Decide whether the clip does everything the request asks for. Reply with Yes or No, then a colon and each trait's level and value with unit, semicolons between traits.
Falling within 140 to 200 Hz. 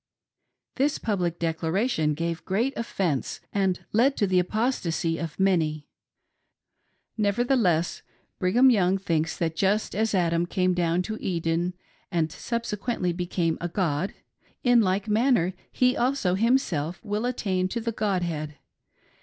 Yes: medium, 185 Hz